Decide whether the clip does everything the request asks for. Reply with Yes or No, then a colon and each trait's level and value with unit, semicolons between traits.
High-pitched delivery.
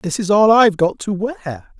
Yes: high, 195 Hz